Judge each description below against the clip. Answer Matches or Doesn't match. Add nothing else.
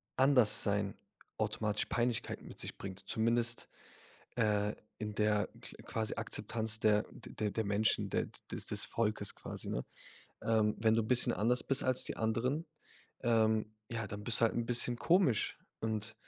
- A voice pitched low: Matches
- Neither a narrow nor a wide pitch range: Doesn't match